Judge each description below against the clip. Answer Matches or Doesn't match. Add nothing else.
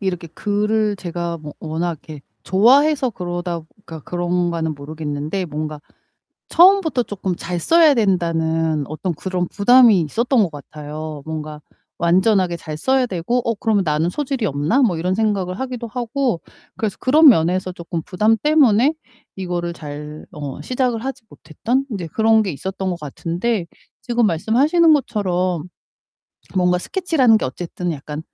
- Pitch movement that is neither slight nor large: Doesn't match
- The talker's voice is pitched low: Doesn't match